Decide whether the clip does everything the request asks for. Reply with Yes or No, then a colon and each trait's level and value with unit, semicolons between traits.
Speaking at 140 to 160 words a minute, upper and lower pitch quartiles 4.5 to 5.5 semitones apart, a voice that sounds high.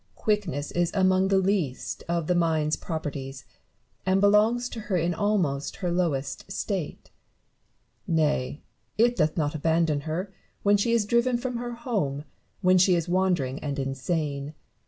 No: average, 155 wpm; average, 5.2 semitones; medium, 175 Hz